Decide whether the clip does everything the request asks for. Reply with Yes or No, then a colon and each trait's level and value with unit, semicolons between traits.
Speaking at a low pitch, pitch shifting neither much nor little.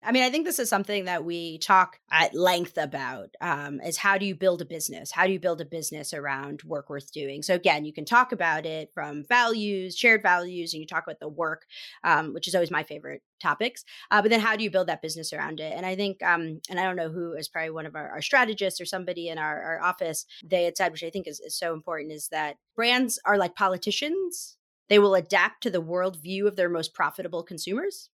No: medium, 175 Hz; average, 3.8 semitones